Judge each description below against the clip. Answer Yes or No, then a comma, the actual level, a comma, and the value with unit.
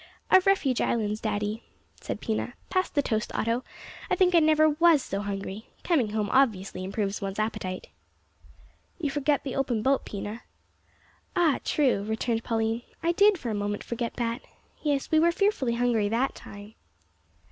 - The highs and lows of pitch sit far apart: Yes, wide, 5.8 semitones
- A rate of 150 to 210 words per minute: Yes, average, 160 wpm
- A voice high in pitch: Yes, high, 235 Hz